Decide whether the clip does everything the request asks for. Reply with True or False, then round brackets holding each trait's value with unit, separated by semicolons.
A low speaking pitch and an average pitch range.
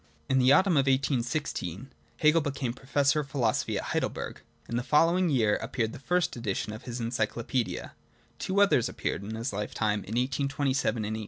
True (130 Hz; 4.1 semitones)